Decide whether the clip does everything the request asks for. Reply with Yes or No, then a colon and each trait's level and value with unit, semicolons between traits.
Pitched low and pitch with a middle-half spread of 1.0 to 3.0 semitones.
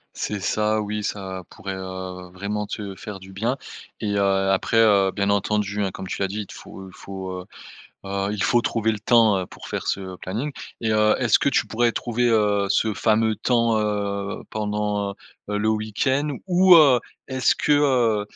Yes: low, 105 Hz; narrow, 2.4 semitones